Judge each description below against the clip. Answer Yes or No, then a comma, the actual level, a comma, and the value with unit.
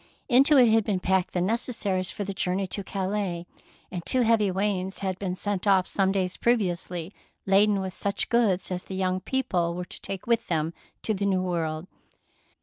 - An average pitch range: No, narrow, 2.3 semitones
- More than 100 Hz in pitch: Yes, high, 190 Hz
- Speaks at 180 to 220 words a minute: Yes, average, 190 wpm